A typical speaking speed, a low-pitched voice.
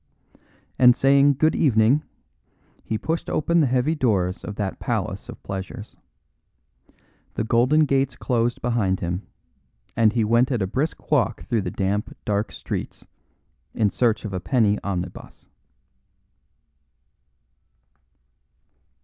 No: slow, 125 wpm; low, 115 Hz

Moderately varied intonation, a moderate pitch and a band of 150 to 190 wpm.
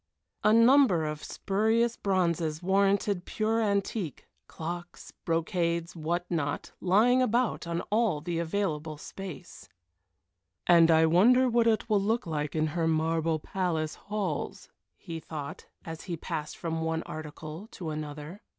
No: average, 4.4 semitones; medium, 170 Hz; slow, 135 wpm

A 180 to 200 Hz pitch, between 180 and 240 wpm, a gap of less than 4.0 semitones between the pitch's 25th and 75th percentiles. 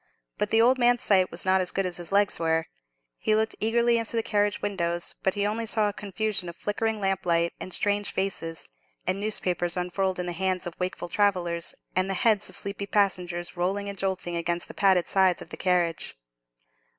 Yes: high, 190 Hz; average, 200 wpm; average, 2.8 semitones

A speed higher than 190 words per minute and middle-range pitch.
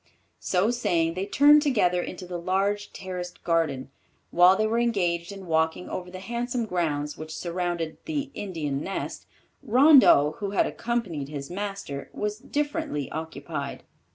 No: average, 145 wpm; medium, 180 Hz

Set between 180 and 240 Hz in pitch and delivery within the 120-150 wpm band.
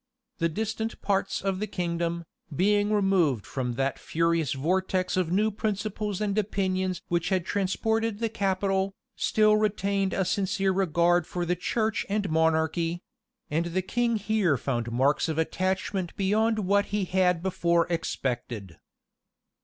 Yes: medium, 185 Hz; average, 140 wpm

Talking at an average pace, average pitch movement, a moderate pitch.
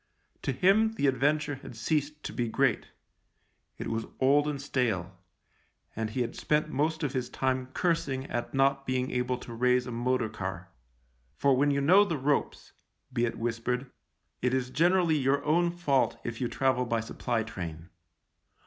No: average, 175 wpm; average, 3.4 semitones; low, 130 Hz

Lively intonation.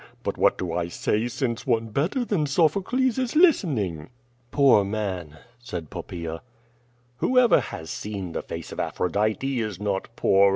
Yes: wide, 8.5 semitones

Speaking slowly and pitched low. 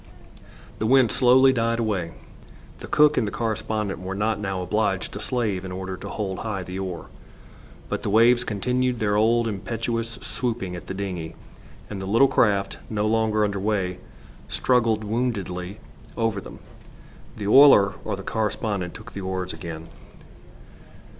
No: average, 155 wpm; low, 105 Hz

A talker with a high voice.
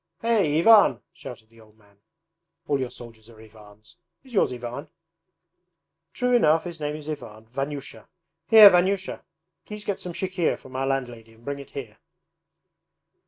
No: medium, 140 Hz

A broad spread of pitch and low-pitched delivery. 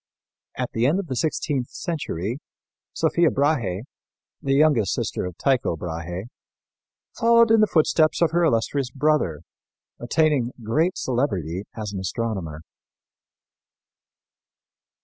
Yes: wide, 8.1 semitones; low, 130 Hz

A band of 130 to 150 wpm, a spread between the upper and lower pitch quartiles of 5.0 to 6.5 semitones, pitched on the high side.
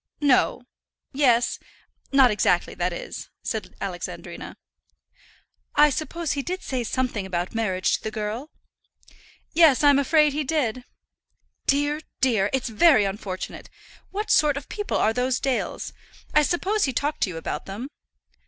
Yes: average, 145 wpm; average, 5.3 semitones; very high, 265 Hz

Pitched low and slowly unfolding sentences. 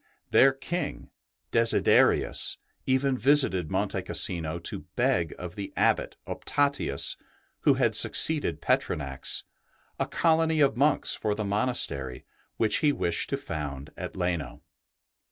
Yes: low, 105 Hz; slow, 125 wpm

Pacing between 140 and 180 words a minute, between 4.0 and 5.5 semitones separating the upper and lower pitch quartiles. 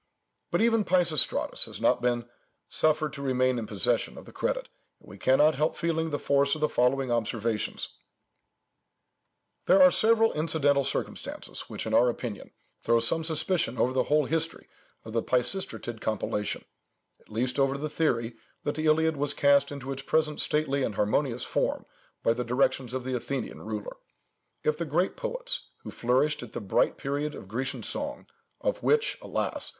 Yes: average, 170 wpm; average, 4.4 semitones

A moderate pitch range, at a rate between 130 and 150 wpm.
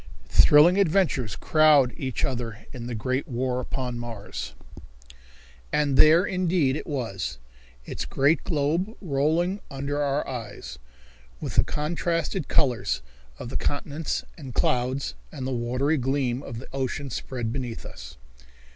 Yes: average, 3.9 semitones; slow, 135 wpm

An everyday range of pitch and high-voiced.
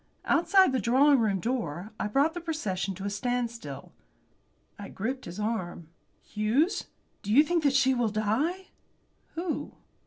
No: wide, 5.9 semitones; high, 240 Hz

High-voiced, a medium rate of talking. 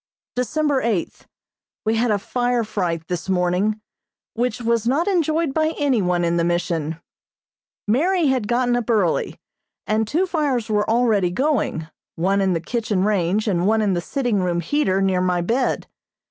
Yes: high, 215 Hz; average, 165 wpm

